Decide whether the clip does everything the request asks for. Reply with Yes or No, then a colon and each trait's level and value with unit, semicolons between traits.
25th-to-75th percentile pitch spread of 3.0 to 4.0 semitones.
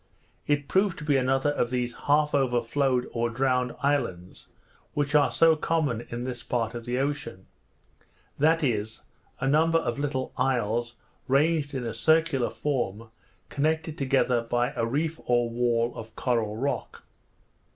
Yes: average, 3.6 semitones